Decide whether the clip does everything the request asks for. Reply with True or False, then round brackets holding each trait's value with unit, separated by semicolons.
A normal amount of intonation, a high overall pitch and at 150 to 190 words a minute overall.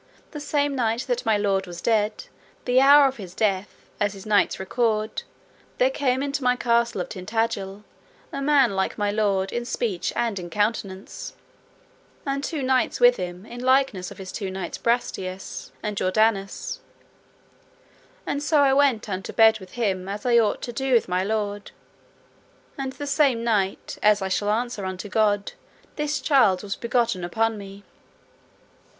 True (4.3 semitones; 220 Hz; 165 wpm)